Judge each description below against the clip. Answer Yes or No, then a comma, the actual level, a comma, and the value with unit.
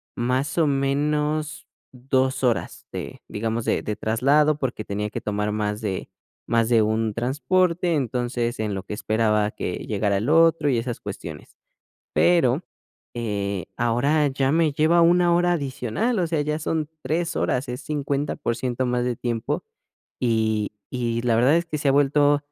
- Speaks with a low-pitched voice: Yes, low, 130 Hz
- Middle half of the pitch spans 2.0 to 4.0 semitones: No, average, 5.1 semitones